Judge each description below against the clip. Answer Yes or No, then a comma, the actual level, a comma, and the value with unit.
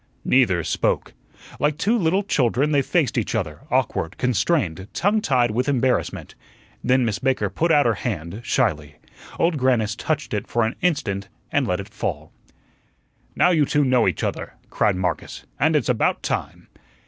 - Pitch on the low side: Yes, low, 125 Hz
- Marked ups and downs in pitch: Yes, wide, 6.5 semitones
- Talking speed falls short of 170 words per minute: Yes, average, 160 wpm